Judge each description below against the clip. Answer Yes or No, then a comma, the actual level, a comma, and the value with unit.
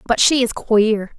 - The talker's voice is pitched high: Yes, high, 225 Hz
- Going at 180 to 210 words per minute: Yes, fast, 205 wpm